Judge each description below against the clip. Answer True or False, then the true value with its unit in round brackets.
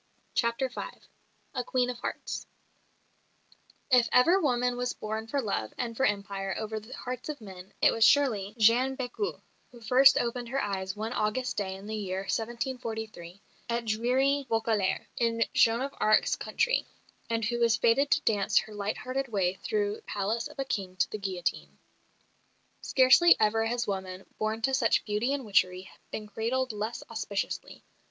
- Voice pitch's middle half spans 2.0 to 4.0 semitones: True (3.4 semitones)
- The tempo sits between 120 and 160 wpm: False (170 wpm)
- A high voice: True (230 Hz)